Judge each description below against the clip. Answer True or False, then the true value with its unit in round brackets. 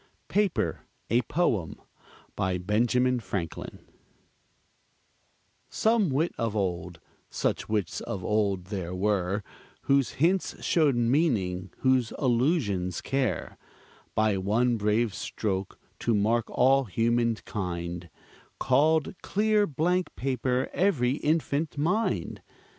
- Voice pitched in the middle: False (115 Hz)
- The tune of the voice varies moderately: False (6.2 semitones)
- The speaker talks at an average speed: False (105 wpm)